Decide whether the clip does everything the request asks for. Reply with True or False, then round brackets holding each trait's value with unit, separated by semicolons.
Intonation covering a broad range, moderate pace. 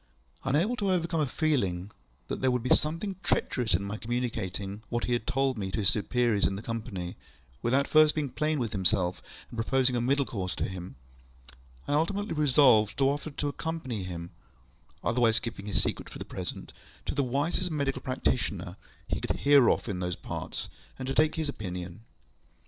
True (6.1 semitones; 185 wpm)